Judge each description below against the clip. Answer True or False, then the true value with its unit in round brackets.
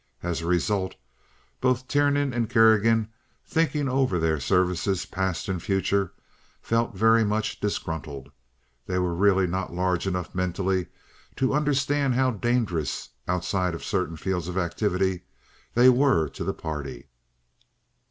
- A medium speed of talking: False (125 wpm)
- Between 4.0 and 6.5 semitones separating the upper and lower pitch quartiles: True (5.1 semitones)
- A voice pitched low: True (95 Hz)